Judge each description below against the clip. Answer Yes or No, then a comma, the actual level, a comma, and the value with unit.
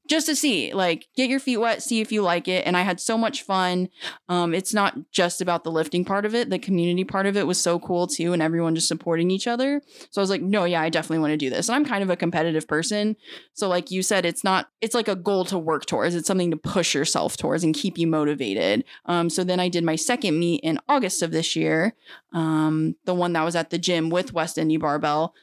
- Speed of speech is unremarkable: No, fast, 260 wpm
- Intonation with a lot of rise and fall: No, average, 3.4 semitones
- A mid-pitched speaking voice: Yes, medium, 175 Hz